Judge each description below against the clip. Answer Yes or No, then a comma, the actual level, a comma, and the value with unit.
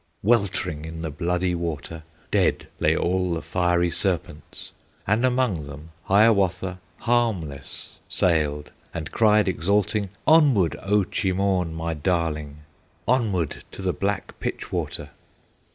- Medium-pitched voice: No, very low, 90 Hz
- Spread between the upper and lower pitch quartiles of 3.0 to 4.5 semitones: Yes, average, 3.9 semitones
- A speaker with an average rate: No, slow, 120 wpm